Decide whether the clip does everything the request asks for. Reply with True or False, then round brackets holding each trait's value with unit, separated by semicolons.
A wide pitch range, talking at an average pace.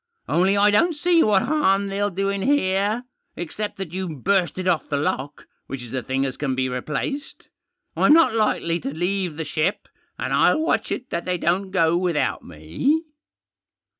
False (5.0 semitones; 180 wpm)